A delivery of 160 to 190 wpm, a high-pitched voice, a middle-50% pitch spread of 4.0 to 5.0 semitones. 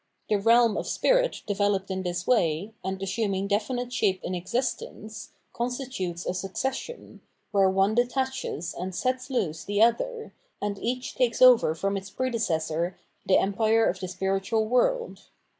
No: average, 145 wpm; high, 205 Hz; average, 4.7 semitones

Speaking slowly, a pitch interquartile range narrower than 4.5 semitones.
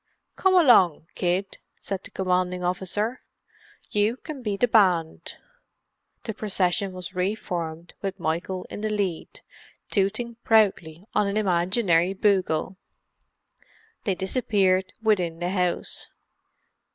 Yes: slow, 115 wpm; average, 2.9 semitones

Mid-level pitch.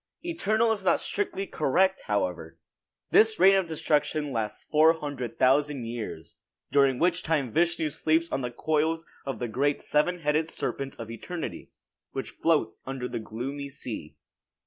Yes: medium, 150 Hz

